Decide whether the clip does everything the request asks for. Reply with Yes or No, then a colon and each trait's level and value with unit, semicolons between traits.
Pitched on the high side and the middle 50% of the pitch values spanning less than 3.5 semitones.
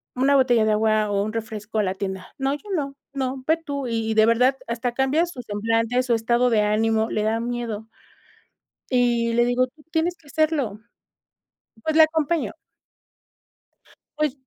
No: high, 240 Hz; average, 4.0 semitones